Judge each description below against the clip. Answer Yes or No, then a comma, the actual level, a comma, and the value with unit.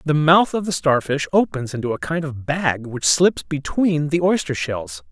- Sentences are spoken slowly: No, average, 200 wpm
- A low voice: No, medium, 150 Hz